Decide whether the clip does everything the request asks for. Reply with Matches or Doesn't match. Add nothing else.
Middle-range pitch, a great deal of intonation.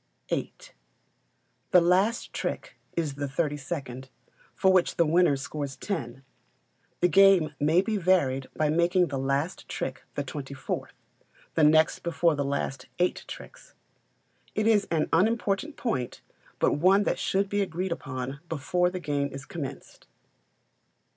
Doesn't match